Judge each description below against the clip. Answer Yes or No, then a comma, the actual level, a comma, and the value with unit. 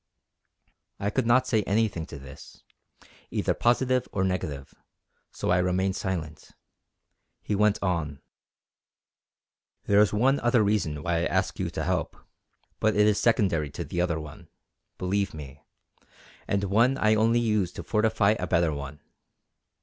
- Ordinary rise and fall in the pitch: Yes, average, 4.8 semitones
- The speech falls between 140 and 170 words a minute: Yes, average, 150 wpm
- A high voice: No, low, 100 Hz